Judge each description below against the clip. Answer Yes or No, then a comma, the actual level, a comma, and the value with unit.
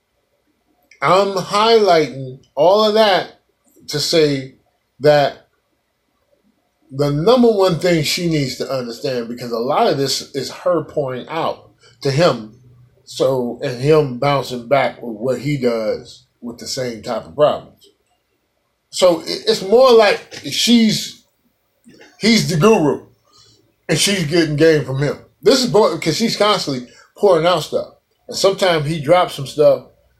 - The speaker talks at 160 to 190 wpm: No, average, 140 wpm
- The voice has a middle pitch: Yes, medium, 150 Hz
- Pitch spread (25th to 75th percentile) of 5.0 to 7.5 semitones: Yes, wide, 5.6 semitones